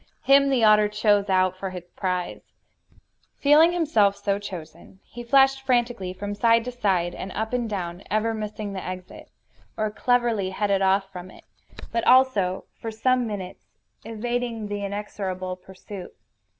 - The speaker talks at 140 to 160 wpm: Yes, average, 150 wpm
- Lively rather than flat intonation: No, average, 3.9 semitones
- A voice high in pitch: Yes, high, 205 Hz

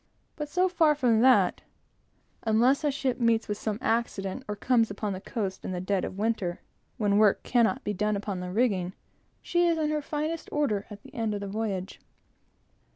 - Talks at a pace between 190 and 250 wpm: Yes, average, 195 wpm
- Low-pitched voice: No, high, 220 Hz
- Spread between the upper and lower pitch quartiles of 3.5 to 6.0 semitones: Yes, average, 4.7 semitones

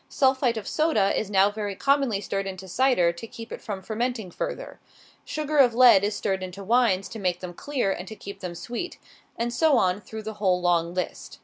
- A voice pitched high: Yes, high, 210 Hz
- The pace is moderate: No, fast, 210 wpm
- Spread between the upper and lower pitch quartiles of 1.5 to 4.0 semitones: No, average, 4.5 semitones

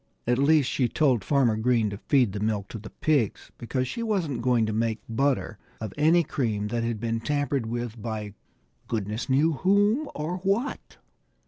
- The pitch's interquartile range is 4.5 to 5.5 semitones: Yes, average, 5.1 semitones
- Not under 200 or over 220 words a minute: No, average, 180 wpm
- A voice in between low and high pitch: No, low, 120 Hz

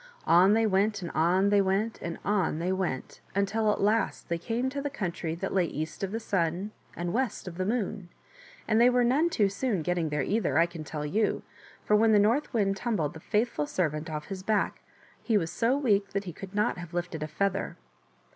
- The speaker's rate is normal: No, fast, 220 wpm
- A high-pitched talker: Yes, high, 195 Hz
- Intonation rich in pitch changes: No, average, 4.2 semitones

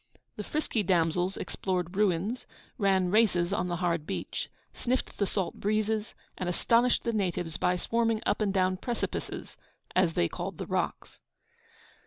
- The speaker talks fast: No, average, 150 wpm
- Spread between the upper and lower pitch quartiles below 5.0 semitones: Yes, average, 3.4 semitones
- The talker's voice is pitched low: No, high, 190 Hz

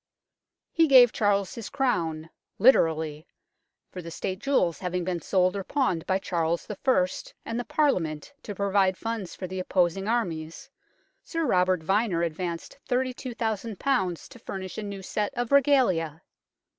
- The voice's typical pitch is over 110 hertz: Yes, high, 190 Hz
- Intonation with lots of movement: Yes, wide, 5.7 semitones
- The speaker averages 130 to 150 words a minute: Yes, average, 145 wpm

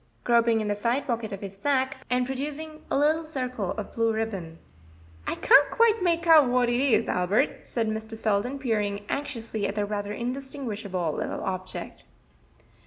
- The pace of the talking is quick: No, average, 170 wpm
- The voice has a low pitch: No, high, 235 Hz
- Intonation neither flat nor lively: Yes, average, 5.0 semitones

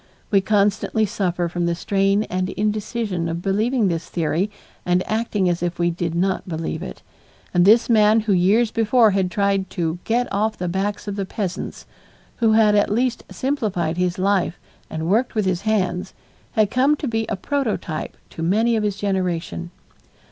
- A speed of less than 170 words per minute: No, average, 175 wpm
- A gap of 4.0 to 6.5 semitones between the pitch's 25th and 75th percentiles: No, average, 3.6 semitones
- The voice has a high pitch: Yes, high, 195 Hz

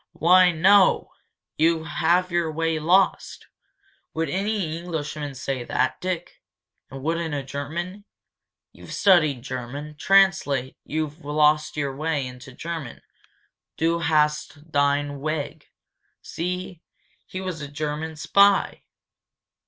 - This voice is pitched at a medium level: Yes, medium, 160 Hz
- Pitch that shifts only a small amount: No, average, 3.2 semitones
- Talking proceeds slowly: Yes, slow, 120 wpm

